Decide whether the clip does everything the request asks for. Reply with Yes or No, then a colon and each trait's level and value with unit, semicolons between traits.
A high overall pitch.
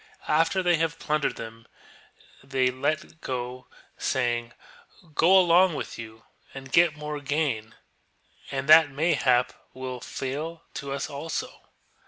No: medium, 140 Hz